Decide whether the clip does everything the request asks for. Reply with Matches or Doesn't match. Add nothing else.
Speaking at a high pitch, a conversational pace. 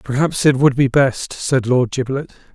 Doesn't match